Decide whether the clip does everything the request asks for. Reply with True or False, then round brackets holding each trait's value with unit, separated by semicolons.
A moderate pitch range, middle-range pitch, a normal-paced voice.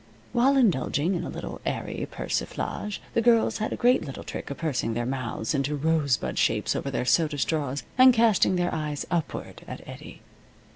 False (7.7 semitones; 160 Hz; 180 wpm)